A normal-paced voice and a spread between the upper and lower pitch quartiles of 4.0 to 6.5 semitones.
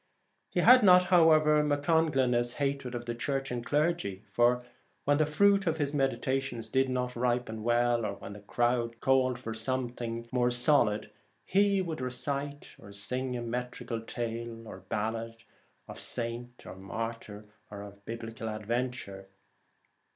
No: average, 150 wpm; average, 3.3 semitones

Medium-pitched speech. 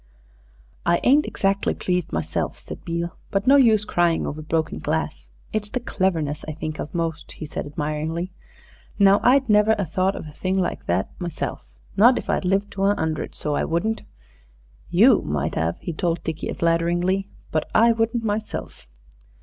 Yes: medium, 175 Hz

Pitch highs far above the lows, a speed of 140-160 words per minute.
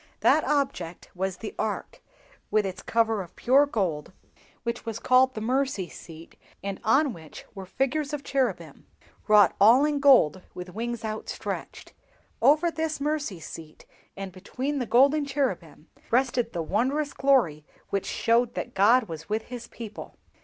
Yes: wide, 6.0 semitones; average, 155 wpm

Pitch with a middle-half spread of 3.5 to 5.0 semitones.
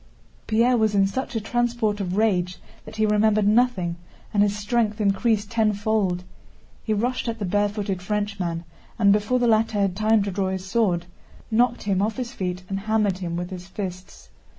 No: narrow, 2.6 semitones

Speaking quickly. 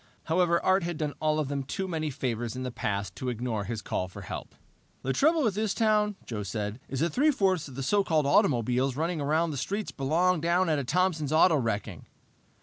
Yes: fast, 215 wpm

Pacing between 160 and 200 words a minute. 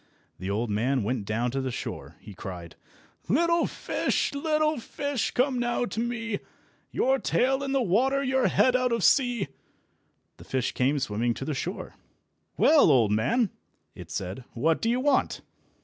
Yes: average, 165 wpm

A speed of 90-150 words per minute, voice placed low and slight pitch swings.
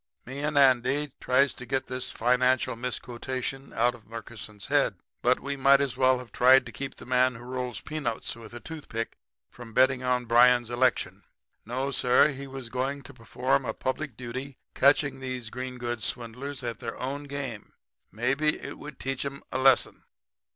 No: average, 180 wpm; low, 130 Hz; narrow, 2.0 semitones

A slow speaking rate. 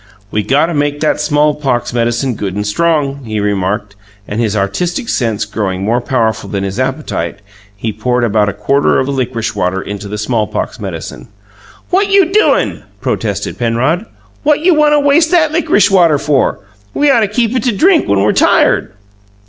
No: average, 180 wpm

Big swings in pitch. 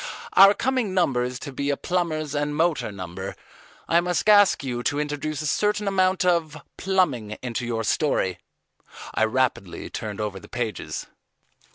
Yes: wide, 6.8 semitones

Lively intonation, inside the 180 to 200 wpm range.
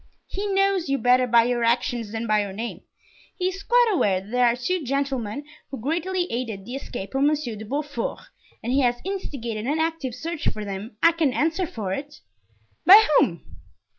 Yes: wide, 6.0 semitones; average, 190 wpm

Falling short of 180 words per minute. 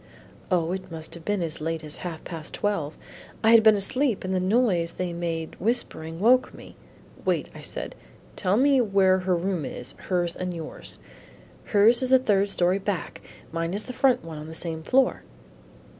No: average, 185 wpm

